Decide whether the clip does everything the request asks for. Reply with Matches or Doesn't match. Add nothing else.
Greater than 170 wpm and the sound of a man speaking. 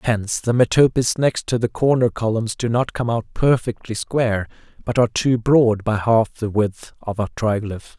Matches